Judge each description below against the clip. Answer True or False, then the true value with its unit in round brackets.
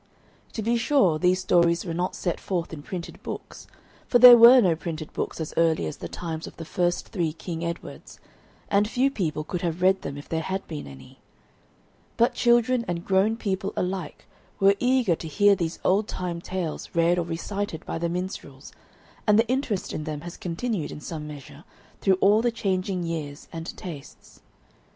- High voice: False (180 Hz)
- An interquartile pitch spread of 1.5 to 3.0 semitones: False (3.8 semitones)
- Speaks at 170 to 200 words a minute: True (190 wpm)